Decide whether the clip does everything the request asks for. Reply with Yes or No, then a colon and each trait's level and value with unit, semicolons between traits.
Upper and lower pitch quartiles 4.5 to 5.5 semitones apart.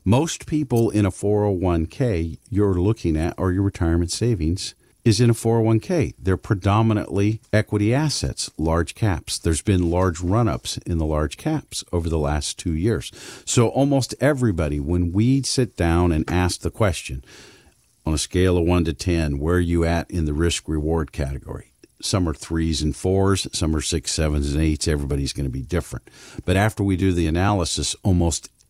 Yes: average, 5.0 semitones